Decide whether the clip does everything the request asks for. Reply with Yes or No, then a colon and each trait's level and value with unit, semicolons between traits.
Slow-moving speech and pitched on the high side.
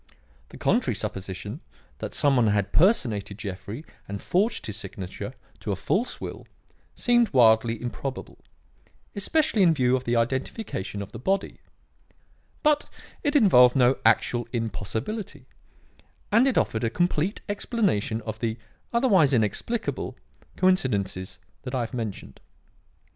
No: slow, 130 wpm; low, 125 Hz